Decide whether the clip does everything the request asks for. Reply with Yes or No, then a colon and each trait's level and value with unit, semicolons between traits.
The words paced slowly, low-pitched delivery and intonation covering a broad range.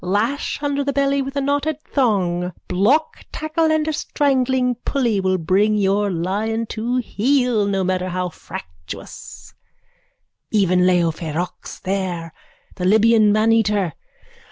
No: slow, 130 wpm; high, 210 Hz; wide, 6.5 semitones